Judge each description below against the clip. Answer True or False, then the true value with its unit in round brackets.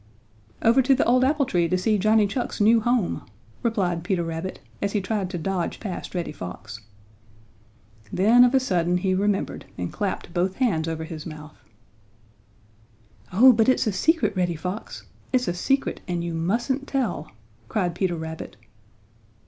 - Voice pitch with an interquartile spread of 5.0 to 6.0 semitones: True (5.3 semitones)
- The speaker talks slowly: False (165 wpm)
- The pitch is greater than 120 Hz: True (190 Hz)